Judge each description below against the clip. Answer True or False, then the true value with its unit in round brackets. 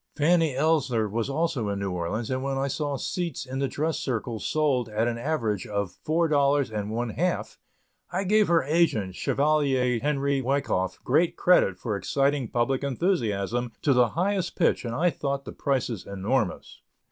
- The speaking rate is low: False (170 wpm)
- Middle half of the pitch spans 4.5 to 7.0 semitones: True (5.2 semitones)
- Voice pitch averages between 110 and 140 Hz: True (135 Hz)